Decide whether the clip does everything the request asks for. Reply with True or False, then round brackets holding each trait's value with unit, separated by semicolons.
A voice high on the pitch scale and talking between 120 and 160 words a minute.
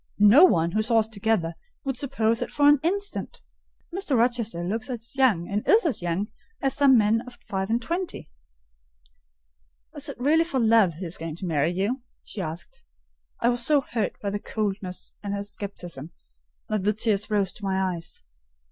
False (220 Hz; 185 wpm)